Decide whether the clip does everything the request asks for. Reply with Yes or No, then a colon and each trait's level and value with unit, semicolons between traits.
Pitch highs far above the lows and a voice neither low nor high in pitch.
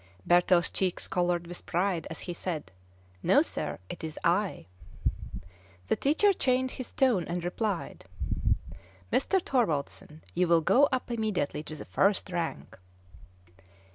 Yes: wide, 5.7 semitones; medium, 180 Hz